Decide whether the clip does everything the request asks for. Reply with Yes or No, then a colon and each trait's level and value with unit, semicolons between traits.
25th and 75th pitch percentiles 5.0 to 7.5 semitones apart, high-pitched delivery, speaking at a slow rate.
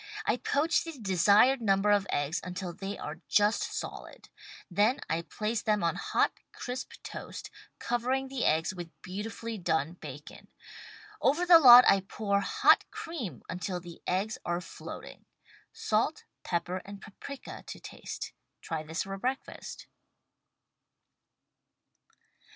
Yes: wide, 5.4 semitones; high, 200 Hz; slow, 130 wpm